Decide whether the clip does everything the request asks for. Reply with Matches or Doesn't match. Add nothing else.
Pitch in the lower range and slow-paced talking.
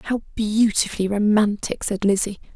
Doesn't match